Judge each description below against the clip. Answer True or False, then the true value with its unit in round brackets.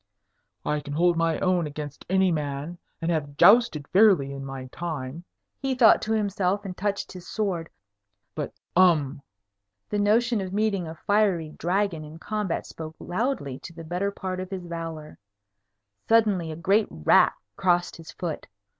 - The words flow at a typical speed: True (160 wpm)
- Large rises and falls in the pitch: False (4.3 semitones)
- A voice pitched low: False (175 Hz)